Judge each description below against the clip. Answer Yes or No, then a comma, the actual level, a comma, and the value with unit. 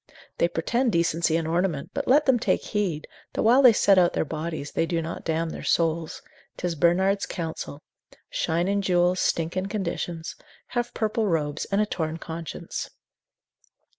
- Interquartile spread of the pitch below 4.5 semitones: Yes, average, 3.6 semitones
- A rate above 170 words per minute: No, average, 165 wpm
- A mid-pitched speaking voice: Yes, medium, 170 Hz